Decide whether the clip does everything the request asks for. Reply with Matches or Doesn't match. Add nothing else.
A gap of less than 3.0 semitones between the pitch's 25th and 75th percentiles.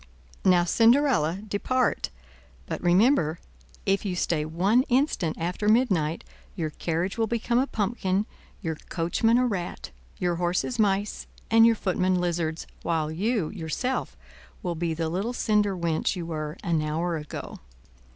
Doesn't match